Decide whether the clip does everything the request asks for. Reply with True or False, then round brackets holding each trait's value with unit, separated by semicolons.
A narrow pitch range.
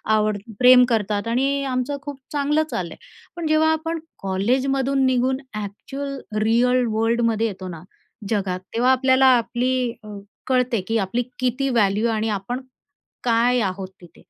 False (3.7 semitones)